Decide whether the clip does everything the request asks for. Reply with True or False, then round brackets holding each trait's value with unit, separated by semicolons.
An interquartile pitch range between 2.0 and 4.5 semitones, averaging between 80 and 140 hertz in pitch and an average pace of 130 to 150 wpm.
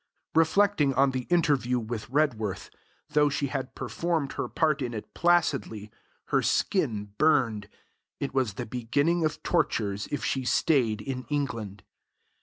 False (5.4 semitones; 135 Hz; 140 wpm)